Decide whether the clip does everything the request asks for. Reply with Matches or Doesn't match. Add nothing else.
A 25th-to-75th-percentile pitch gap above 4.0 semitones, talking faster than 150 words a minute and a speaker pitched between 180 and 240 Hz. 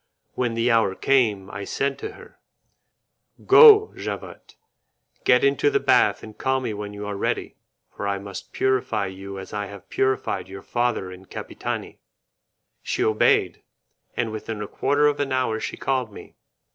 Doesn't match